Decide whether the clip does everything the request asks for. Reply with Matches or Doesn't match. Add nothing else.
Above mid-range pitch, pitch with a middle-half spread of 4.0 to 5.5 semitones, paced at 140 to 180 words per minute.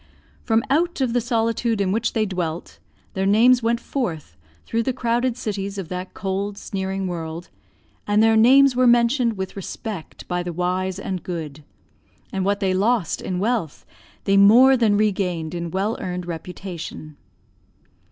Matches